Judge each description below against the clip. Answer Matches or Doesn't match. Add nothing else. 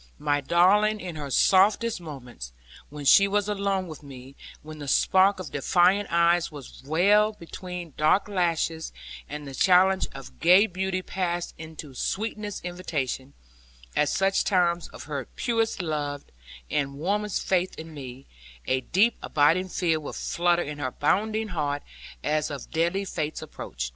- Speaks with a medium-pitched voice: Matches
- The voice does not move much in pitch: Doesn't match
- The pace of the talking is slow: Doesn't match